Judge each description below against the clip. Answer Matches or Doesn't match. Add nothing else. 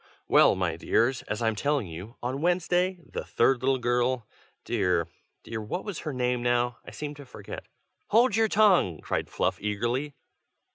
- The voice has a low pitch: Matches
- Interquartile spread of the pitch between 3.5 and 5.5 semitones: Matches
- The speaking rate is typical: Matches